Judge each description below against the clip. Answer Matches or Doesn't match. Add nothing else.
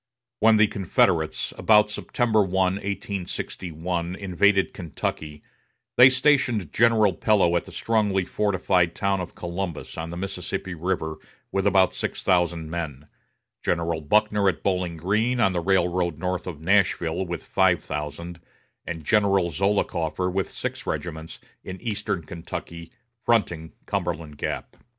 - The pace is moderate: Doesn't match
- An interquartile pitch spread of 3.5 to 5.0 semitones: Doesn't match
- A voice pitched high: Doesn't match